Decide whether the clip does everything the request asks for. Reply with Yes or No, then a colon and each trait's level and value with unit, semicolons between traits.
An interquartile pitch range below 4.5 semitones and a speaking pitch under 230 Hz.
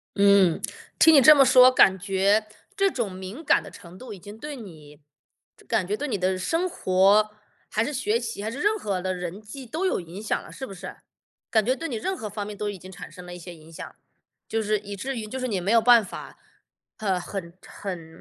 No: average, 5.0 semitones; high, 210 Hz